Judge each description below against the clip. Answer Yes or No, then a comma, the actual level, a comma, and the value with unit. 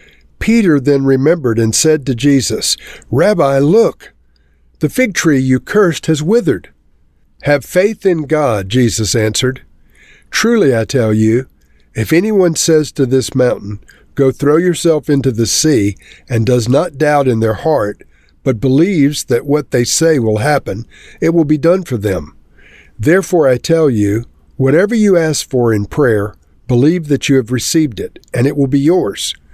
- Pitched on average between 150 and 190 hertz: No, low, 135 Hz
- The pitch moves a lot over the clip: Yes, wide, 5.8 semitones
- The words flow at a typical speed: Yes, average, 165 wpm